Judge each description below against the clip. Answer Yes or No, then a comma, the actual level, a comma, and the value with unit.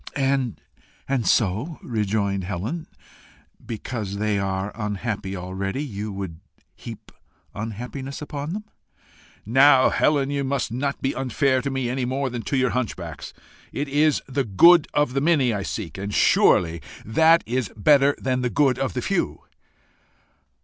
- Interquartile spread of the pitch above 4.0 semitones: Yes, average, 5.3 semitones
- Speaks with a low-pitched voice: Yes, low, 125 Hz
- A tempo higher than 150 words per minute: No, average, 145 wpm